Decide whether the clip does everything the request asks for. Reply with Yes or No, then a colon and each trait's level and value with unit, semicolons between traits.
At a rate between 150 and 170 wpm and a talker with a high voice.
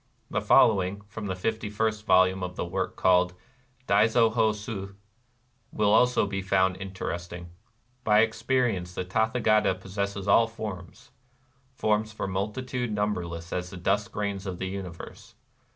No: average, 160 wpm; low, 100 Hz